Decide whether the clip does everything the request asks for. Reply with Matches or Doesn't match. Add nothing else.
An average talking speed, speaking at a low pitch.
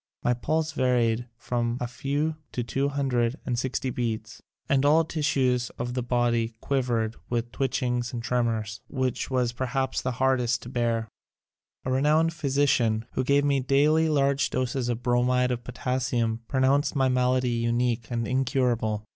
Matches